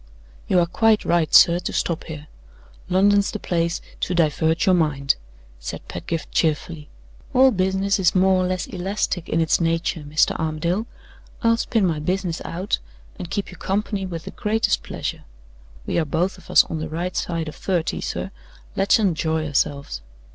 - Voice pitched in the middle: Yes, medium, 175 Hz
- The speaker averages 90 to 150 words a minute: No, average, 170 wpm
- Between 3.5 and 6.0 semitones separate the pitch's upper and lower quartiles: No, average, 3.1 semitones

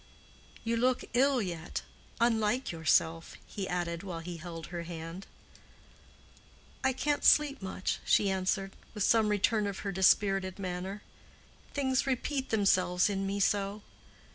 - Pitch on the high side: Yes, high, 195 Hz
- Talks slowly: Yes, slow, 130 wpm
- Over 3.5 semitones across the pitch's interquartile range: Yes, average, 4.2 semitones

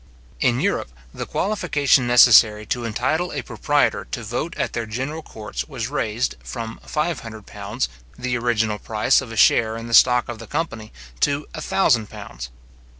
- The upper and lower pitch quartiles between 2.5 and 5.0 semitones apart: Yes, average, 4.3 semitones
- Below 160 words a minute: No, average, 170 wpm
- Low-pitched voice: Yes, low, 120 Hz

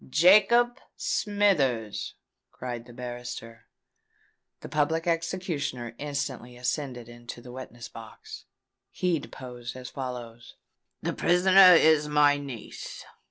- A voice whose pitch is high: No, low, 130 Hz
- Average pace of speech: No, slow, 105 wpm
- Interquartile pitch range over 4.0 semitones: Yes, average, 5.3 semitones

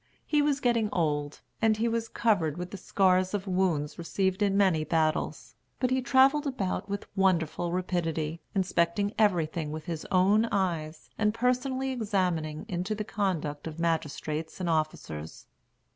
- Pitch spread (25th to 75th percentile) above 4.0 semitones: Yes, average, 4.8 semitones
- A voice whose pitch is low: No, medium, 185 Hz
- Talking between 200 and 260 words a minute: No, average, 150 wpm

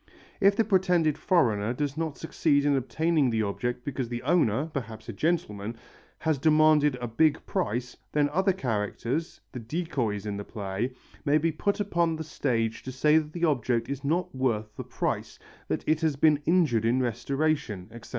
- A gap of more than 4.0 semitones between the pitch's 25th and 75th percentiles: Yes, average, 5.2 semitones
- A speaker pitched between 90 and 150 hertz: Yes, medium, 140 Hz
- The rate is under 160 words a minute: No, average, 180 wpm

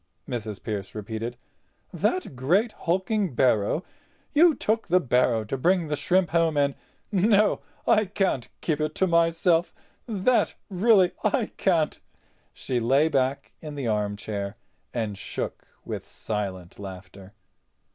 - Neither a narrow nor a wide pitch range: No, wide, 9.0 semitones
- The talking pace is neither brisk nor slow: No, slow, 120 wpm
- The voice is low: No, medium, 150 Hz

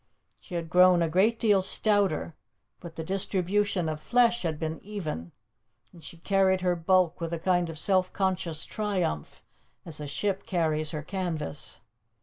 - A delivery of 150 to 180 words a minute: Yes, average, 160 wpm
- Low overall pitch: No, medium, 180 Hz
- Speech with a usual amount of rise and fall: Yes, average, 3.3 semitones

